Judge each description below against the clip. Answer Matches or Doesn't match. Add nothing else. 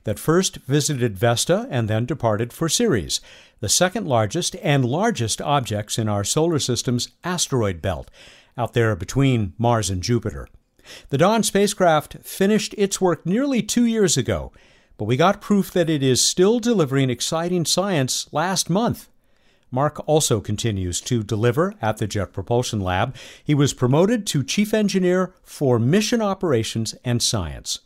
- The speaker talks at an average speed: Matches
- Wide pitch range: Matches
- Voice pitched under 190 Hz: Matches